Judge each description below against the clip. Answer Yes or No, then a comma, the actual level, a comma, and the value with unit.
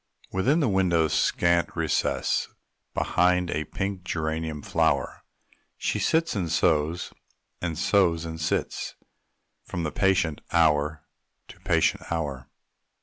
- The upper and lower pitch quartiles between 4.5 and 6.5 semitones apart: No, narrow, 2.6 semitones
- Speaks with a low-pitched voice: Yes, very low, 85 Hz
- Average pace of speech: No, slow, 110 wpm